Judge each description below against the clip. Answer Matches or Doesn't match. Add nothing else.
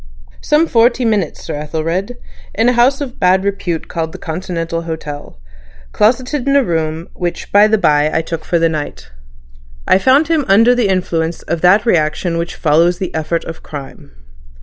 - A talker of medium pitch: Matches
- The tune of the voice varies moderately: Doesn't match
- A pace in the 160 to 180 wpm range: Matches